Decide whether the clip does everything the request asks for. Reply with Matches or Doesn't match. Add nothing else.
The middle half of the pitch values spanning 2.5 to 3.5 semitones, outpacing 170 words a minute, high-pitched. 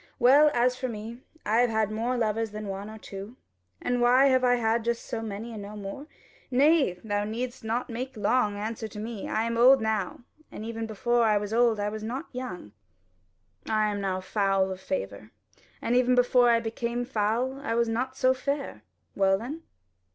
Matches